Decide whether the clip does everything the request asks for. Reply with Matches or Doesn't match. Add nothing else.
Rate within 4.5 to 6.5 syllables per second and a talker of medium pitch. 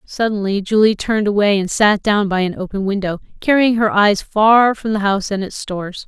Doesn't match